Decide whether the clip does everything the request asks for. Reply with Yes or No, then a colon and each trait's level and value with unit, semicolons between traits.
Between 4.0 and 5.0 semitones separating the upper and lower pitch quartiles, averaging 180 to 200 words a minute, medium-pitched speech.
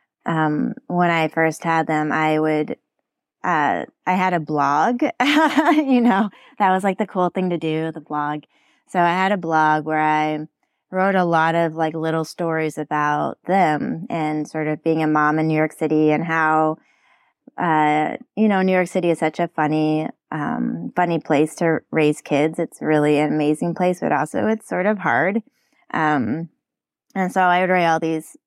No: average, 3.0 semitones; average, 185 wpm; medium, 160 Hz